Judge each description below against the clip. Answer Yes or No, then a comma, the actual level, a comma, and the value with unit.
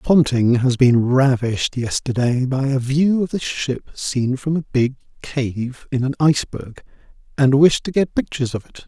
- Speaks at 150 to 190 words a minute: Yes, average, 175 wpm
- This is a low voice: Yes, low, 130 Hz